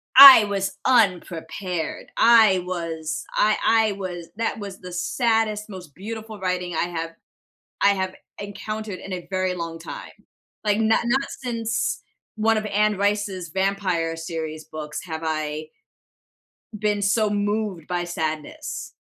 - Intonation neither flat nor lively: Yes, average, 4.1 semitones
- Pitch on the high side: Yes, high, 195 Hz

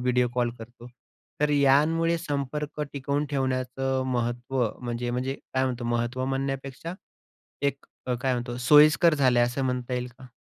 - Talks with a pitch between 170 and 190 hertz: No, low, 130 Hz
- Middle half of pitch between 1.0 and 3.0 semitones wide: Yes, narrow, 2.4 semitones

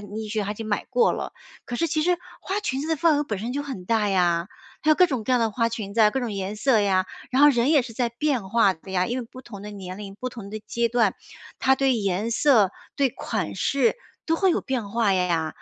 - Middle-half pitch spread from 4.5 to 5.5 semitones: Yes, average, 4.9 semitones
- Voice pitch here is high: Yes, high, 230 Hz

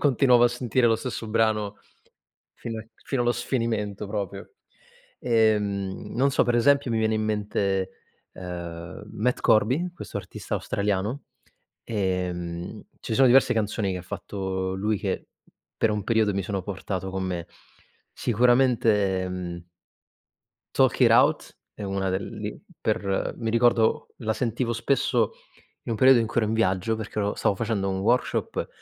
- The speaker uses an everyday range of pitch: Yes, average, 3.5 semitones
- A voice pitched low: Yes, low, 105 Hz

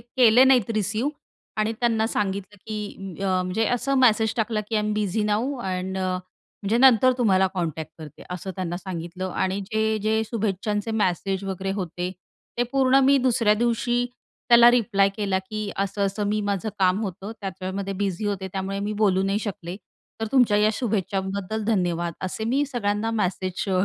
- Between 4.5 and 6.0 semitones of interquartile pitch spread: No, average, 2.8 semitones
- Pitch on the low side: No, high, 205 Hz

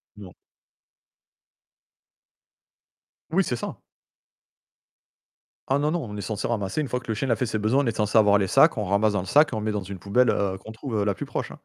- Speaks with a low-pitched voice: Yes, low, 110 Hz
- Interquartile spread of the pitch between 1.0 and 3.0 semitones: No, average, 3.8 semitones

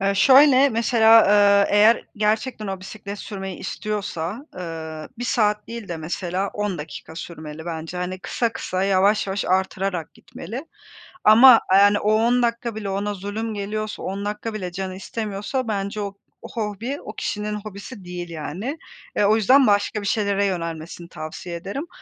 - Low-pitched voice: No, high, 205 Hz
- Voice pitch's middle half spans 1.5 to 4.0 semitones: Yes, average, 2.9 semitones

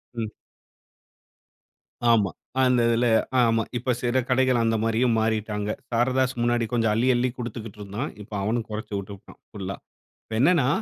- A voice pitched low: Yes, low, 115 Hz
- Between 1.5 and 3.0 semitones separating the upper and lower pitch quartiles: Yes, narrow, 2.5 semitones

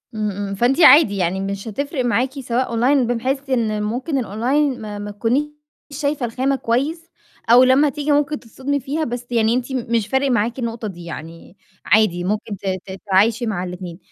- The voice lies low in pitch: No, high, 235 Hz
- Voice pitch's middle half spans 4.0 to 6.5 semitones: Yes, average, 4.6 semitones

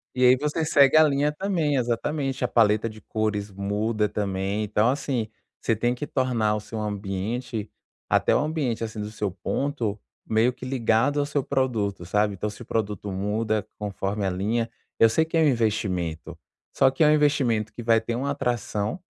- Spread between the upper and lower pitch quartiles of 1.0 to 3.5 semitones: No, average, 4.3 semitones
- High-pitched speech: No, low, 115 Hz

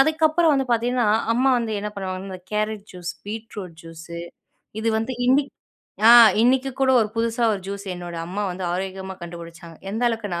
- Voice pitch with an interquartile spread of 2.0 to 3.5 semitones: No, average, 4.9 semitones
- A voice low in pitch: No, high, 210 Hz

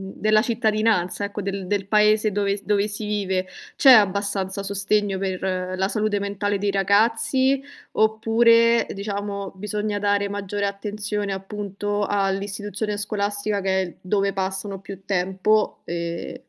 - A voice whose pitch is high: Yes, high, 205 Hz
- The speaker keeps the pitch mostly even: Yes, narrow, 1.4 semitones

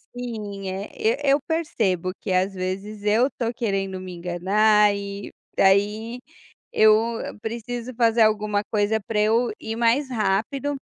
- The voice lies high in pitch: Yes, high, 215 Hz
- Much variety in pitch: No, average, 2.9 semitones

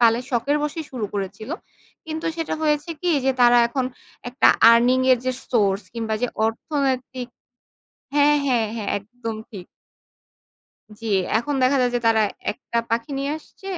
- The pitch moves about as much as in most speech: Yes, average, 3.8 semitones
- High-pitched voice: Yes, high, 245 Hz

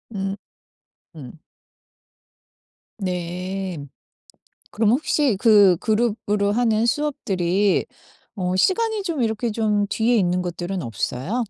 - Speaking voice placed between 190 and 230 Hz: Yes, high, 205 Hz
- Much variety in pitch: No, average, 4.3 semitones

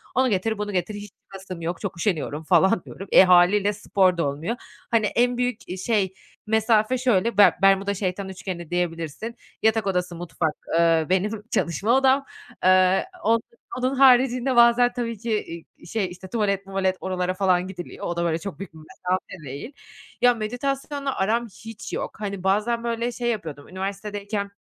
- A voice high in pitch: Yes, high, 200 Hz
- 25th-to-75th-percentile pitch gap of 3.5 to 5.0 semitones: Yes, average, 4.0 semitones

